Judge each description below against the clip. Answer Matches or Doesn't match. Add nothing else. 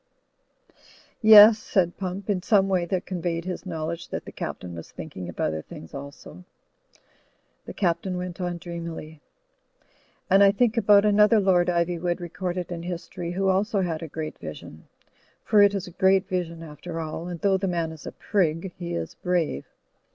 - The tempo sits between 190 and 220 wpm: Doesn't match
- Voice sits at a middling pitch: Matches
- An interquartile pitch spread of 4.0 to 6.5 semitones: Doesn't match